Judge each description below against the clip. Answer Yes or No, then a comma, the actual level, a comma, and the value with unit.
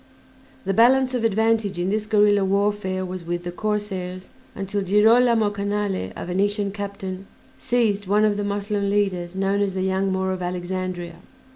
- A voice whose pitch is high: Yes, high, 200 Hz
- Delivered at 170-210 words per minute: No, average, 160 wpm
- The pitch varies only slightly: Yes, narrow, 1.8 semitones